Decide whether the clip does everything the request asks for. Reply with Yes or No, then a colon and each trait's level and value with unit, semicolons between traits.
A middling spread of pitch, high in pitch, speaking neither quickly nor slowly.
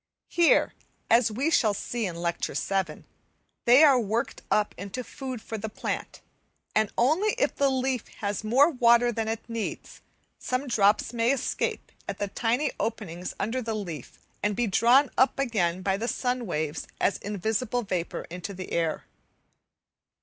Yes: average, 4.2 semitones; high, 225 Hz; average, 160 wpm